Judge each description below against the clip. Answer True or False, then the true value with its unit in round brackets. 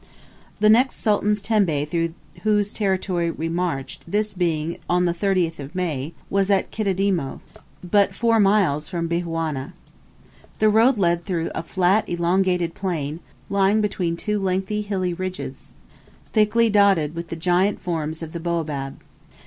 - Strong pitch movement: False (3.5 semitones)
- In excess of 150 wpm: False (140 wpm)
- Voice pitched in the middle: True (180 Hz)